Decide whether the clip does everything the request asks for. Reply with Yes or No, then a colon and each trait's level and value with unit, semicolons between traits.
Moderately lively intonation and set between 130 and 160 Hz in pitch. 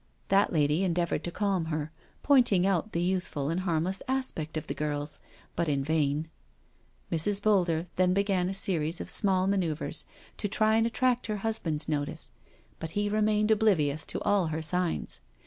No: average, 4.5 semitones; medium, 180 Hz